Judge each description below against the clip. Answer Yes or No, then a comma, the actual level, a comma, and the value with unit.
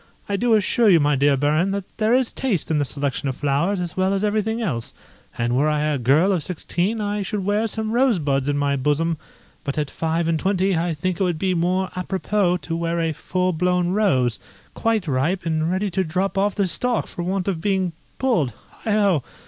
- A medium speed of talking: No, fast, 215 wpm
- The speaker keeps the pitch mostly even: No, average, 4.8 semitones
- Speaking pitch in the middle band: Yes, medium, 180 Hz